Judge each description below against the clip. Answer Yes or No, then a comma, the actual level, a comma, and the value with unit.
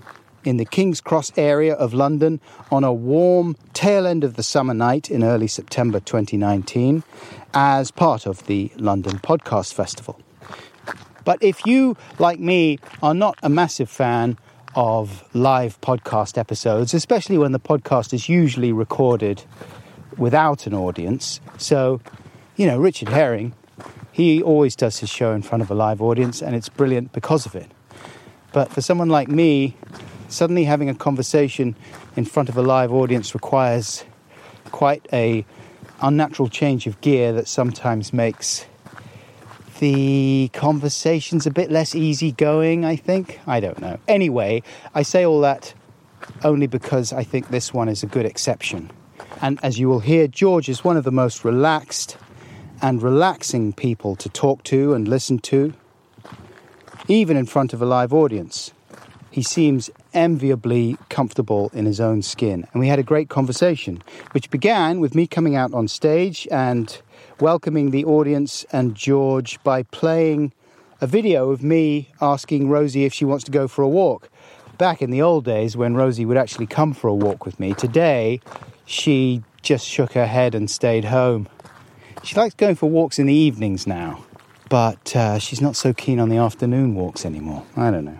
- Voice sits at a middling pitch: No, low, 130 Hz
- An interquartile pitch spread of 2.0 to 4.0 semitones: No, average, 4.5 semitones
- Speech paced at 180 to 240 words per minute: No, average, 165 wpm